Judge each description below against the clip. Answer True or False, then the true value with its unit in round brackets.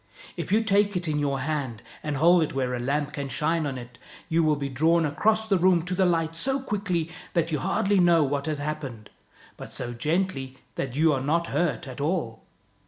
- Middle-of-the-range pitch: True (155 Hz)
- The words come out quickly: True (215 wpm)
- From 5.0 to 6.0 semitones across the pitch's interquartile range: False (4.3 semitones)